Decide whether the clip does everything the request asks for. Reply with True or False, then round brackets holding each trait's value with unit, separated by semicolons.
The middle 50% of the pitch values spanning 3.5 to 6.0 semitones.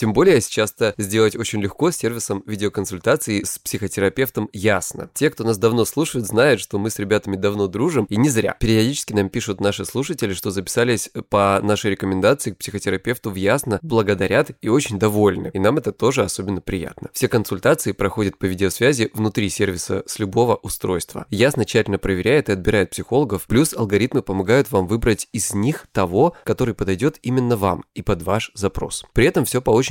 False (2.6 semitones)